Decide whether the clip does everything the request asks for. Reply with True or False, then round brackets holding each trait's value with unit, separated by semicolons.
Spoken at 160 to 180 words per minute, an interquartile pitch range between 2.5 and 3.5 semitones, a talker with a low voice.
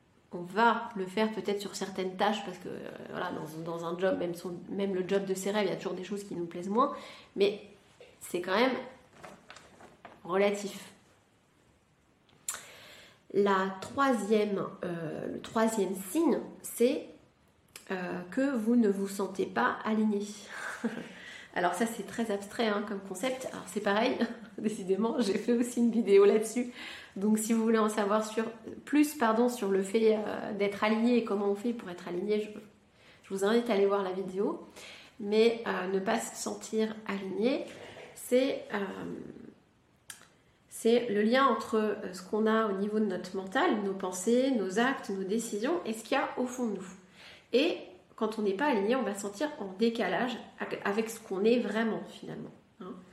False (175 wpm; 3.0 semitones; 215 Hz)